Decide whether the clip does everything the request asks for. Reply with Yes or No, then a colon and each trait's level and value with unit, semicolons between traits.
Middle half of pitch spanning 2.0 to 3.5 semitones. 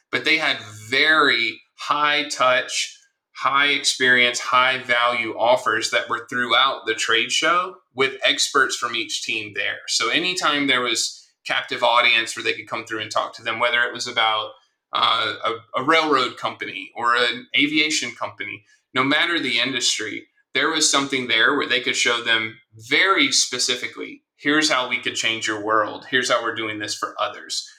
No: average, 4.6 semitones